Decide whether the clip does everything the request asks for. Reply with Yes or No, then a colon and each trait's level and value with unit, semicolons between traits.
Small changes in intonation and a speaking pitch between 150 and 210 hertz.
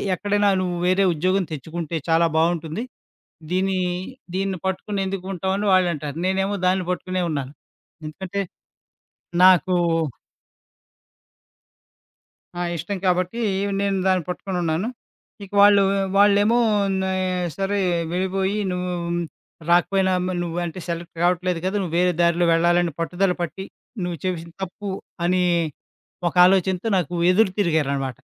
Yes: narrow, 2.0 semitones; medium, 185 Hz